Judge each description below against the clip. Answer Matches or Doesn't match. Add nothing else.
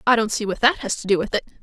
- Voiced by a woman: Matches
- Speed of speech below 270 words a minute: Doesn't match